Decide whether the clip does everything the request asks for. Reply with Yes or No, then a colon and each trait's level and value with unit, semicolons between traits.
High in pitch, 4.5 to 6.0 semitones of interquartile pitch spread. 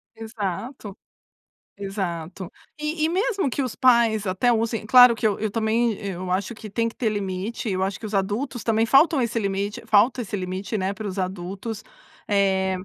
No: high, 215 Hz; average, 3.5 semitones